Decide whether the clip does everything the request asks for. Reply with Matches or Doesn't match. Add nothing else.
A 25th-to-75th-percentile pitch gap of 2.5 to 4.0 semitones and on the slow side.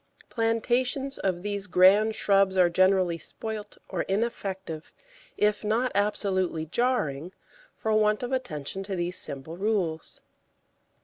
Matches